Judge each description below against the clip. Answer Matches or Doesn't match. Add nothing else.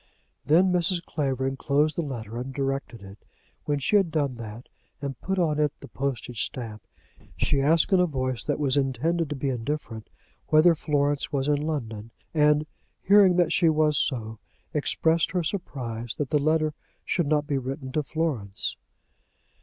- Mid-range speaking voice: Matches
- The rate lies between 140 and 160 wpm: Doesn't match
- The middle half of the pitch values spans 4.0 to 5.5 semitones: Doesn't match